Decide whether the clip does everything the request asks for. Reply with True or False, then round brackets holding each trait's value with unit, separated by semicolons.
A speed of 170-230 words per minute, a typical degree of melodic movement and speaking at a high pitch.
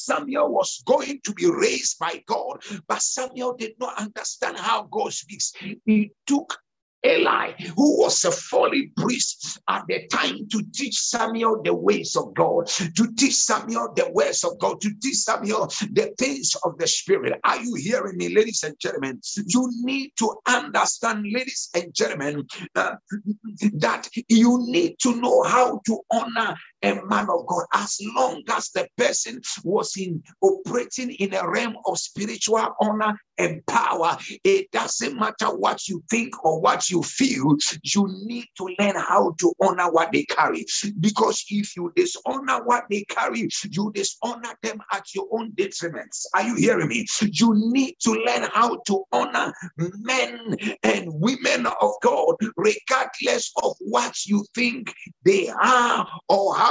False (160 wpm; 4.3 semitones; 225 Hz)